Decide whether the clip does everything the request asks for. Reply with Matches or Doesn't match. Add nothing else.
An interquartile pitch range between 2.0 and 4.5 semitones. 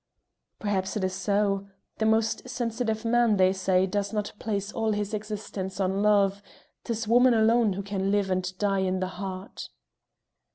Matches